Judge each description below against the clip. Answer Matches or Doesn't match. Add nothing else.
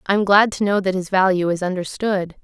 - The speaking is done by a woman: Matches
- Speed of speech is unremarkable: Doesn't match